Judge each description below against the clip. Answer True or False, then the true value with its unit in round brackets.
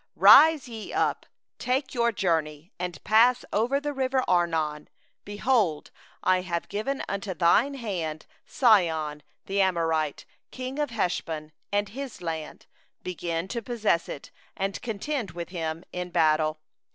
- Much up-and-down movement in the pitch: True (6.3 semitones)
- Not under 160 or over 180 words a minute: False (140 wpm)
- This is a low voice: False (185 Hz)